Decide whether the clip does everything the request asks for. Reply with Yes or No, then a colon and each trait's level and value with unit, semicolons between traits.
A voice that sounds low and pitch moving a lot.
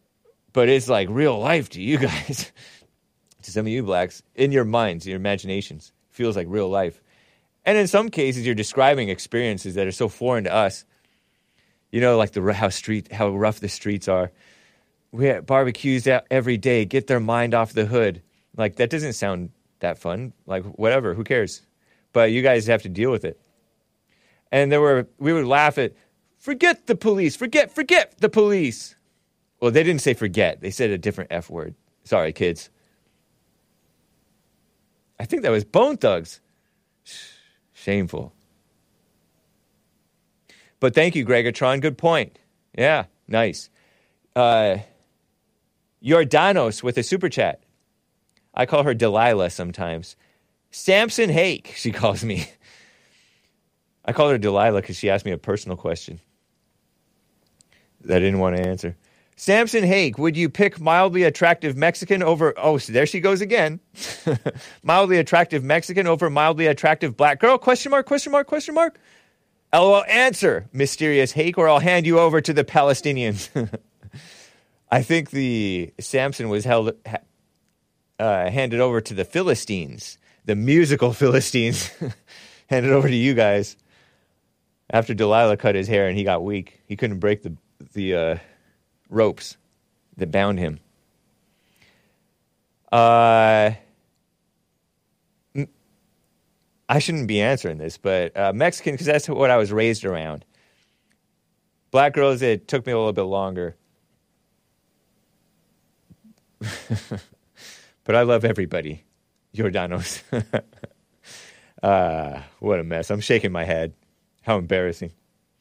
Yes: low, 120 Hz; wide, 7.6 semitones